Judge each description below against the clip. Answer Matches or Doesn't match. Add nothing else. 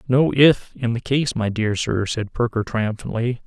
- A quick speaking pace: Doesn't match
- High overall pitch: Doesn't match